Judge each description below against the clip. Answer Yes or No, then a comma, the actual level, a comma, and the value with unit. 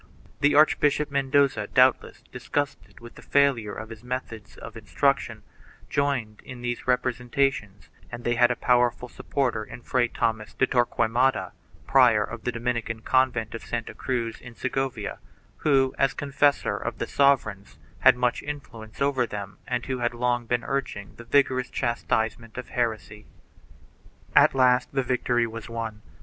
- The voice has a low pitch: Yes, low, 125 Hz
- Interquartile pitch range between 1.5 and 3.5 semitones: Yes, narrow, 2.6 semitones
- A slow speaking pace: No, average, 155 wpm